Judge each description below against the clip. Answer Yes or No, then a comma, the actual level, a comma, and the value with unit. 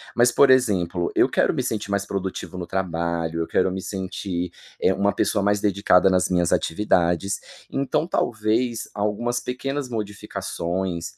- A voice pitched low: Yes, low, 100 Hz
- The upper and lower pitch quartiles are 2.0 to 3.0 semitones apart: No, average, 3.5 semitones